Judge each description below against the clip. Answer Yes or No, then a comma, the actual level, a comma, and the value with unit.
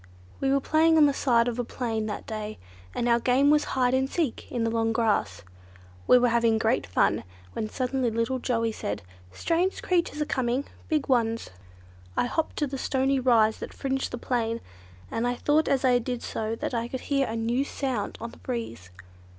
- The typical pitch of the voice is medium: No, high, 245 Hz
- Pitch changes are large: No, average, 2.9 semitones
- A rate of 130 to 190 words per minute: No, fast, 205 wpm